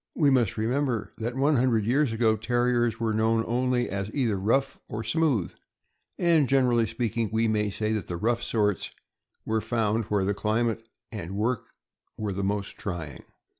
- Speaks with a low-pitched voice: Yes, low, 115 Hz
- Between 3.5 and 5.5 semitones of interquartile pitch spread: No, narrow, 2.6 semitones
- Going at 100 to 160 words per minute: No, average, 170 wpm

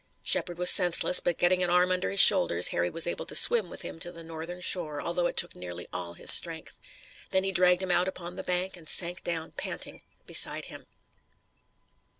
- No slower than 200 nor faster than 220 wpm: Yes, fast, 205 wpm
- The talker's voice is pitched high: No, medium, 175 Hz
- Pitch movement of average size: No, narrow, 1.8 semitones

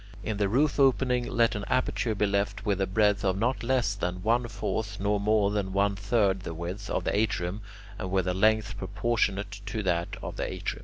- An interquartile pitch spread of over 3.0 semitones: No, narrow, 2.4 semitones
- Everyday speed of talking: No, fast, 210 wpm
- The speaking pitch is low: Yes, low, 105 Hz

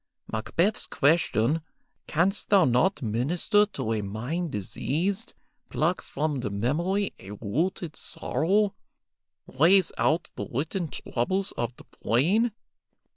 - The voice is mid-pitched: Yes, medium, 160 Hz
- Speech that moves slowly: Yes, slow, 115 wpm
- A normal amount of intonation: No, wide, 7.8 semitones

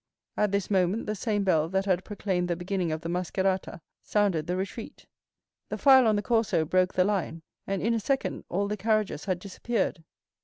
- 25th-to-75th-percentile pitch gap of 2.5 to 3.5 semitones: Yes, average, 2.8 semitones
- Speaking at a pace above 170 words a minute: Yes, average, 195 wpm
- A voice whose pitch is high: Yes, high, 195 Hz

